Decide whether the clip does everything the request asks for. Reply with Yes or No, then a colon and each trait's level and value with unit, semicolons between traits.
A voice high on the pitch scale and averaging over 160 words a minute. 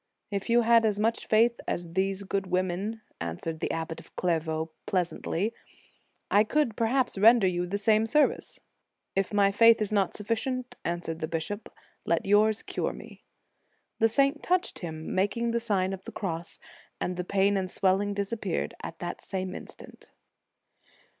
Yes: high, 200 Hz; average, 170 wpm